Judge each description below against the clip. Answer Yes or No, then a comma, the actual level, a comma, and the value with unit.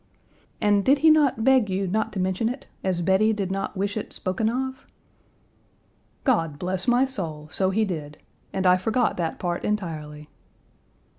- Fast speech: No, average, 165 wpm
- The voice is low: No, high, 195 Hz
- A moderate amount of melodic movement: Yes, average, 3.7 semitones